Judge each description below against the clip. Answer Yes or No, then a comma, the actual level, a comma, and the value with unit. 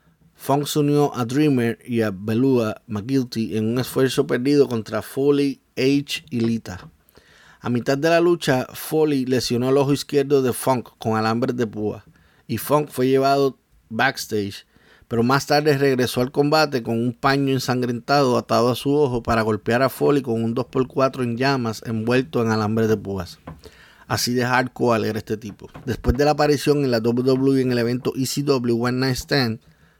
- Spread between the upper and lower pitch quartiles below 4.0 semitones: Yes, average, 3.3 semitones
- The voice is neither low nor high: No, low, 125 Hz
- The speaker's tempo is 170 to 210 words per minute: Yes, average, 175 wpm